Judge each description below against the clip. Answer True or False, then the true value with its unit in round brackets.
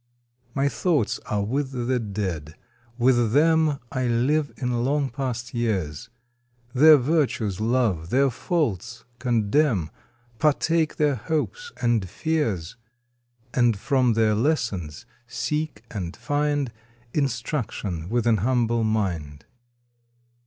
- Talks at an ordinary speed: False (110 wpm)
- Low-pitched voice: True (120 Hz)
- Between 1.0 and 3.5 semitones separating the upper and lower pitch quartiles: False (5.3 semitones)